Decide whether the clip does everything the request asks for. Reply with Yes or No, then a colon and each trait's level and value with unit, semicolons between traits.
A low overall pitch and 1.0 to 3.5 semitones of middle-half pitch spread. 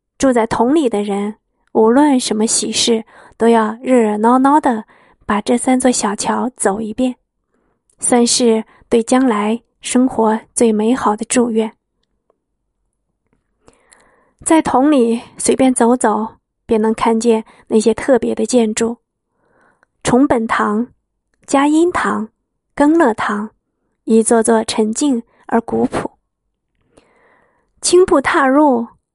No: high, 235 Hz; average, 2.7 semitones